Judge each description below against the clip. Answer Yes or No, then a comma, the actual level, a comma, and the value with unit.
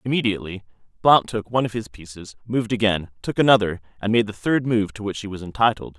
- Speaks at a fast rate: Yes, fast, 210 wpm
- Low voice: Yes, low, 105 Hz